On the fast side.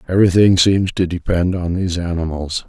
No: average, 155 wpm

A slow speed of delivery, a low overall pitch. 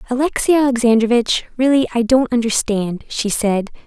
No: slow, 125 wpm; high, 240 Hz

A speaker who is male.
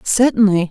No: female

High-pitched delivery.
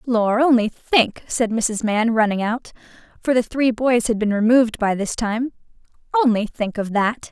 Yes: high, 230 Hz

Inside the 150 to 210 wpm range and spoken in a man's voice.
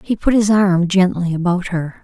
No: fast, 205 wpm; female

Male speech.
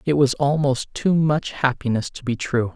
Yes: male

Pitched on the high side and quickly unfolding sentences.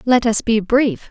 Yes: high, 230 Hz; fast, 220 wpm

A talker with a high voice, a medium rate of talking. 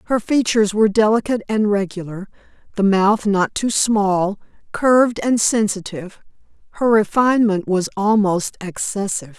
No: high, 205 Hz; slow, 120 wpm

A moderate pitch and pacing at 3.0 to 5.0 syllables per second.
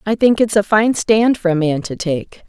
No: high, 200 Hz; 4.7 syllables/s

